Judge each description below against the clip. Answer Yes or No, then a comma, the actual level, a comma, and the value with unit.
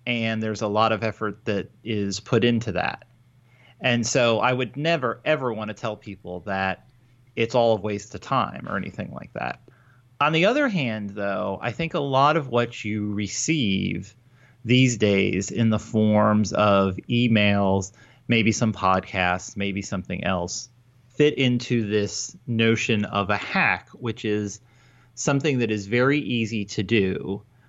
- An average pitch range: Yes, average, 3.1 semitones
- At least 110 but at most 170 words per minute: Yes, average, 160 wpm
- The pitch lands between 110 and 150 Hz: Yes, low, 115 Hz